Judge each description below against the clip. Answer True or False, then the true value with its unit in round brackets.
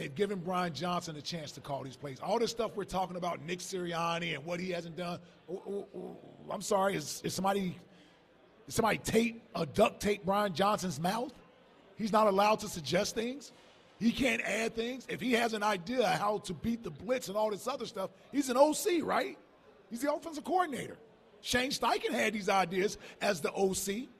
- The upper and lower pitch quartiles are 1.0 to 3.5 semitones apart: False (4.3 semitones)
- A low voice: False (205 Hz)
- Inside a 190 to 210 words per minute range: True (205 wpm)